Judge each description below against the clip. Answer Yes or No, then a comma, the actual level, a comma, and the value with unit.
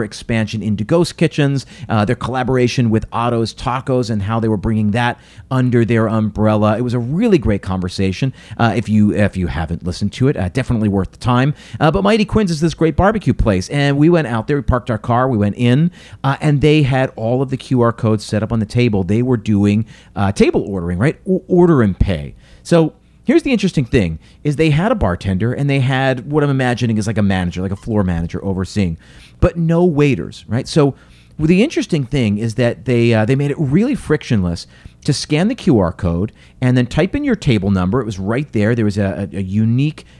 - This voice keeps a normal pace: No, fast, 220 wpm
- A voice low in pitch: Yes, low, 120 Hz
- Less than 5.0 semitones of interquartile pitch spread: No, wide, 5.6 semitones